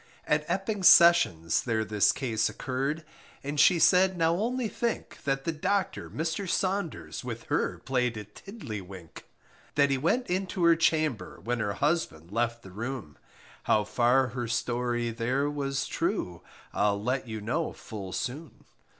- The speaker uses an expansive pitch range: Yes, wide, 6.7 semitones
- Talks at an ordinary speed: Yes, average, 155 wpm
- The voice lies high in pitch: No, low, 135 Hz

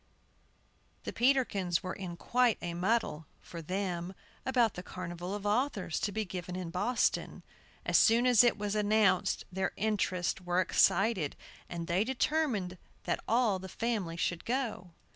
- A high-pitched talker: Yes, high, 195 Hz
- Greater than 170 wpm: No, average, 150 wpm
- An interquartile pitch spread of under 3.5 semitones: No, average, 4.3 semitones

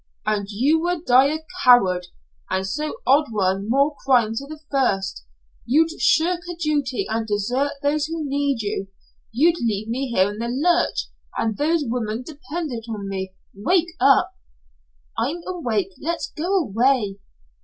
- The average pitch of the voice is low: No, very high, 255 Hz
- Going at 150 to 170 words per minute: Yes, average, 155 wpm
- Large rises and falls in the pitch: Yes, wide, 6.7 semitones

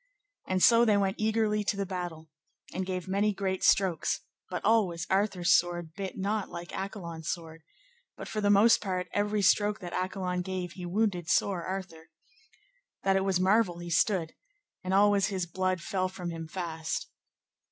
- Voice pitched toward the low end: No, high, 190 Hz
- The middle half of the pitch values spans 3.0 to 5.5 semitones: No, narrow, 2.5 semitones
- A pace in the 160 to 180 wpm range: Yes, average, 170 wpm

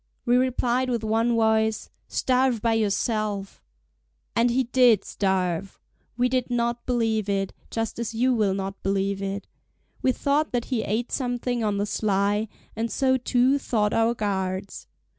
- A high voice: Yes, high, 225 Hz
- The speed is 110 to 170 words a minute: Yes, average, 155 wpm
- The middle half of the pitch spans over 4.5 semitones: No, average, 3.4 semitones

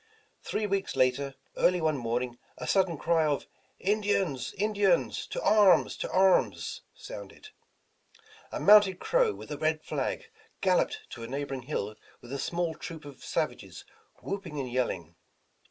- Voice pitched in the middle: Yes, medium, 160 Hz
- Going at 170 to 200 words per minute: No, average, 150 wpm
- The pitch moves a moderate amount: No, wide, 6.9 semitones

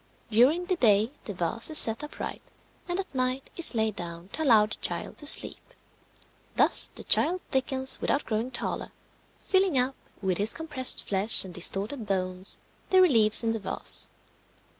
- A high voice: Yes, high, 235 Hz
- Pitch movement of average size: No, wide, 6.4 semitones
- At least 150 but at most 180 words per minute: Yes, average, 165 wpm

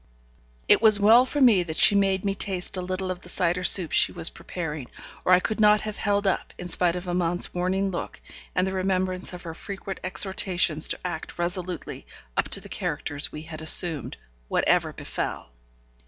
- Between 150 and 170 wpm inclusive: No, average, 190 wpm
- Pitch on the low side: No, medium, 185 Hz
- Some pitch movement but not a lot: No, narrow, 2.0 semitones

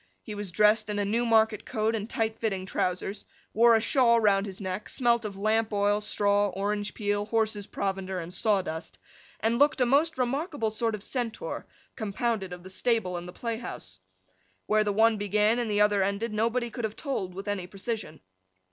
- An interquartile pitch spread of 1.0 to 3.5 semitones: Yes, narrow, 2.5 semitones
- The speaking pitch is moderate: No, high, 210 Hz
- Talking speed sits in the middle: Yes, average, 190 wpm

